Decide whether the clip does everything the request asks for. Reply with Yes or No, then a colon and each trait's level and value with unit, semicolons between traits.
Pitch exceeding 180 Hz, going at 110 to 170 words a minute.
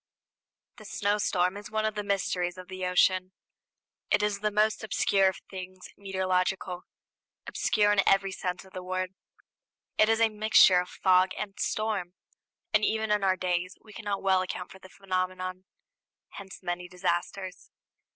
Yes: high, 190 Hz; average, 160 wpm